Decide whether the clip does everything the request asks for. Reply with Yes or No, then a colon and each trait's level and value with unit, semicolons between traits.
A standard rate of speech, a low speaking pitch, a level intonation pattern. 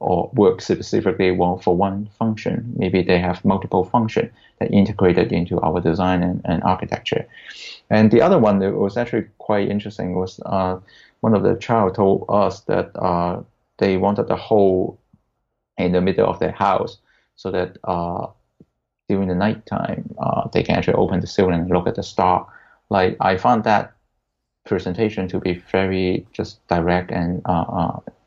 Yes: average, 170 wpm; very low, 95 Hz; narrow, 2.3 semitones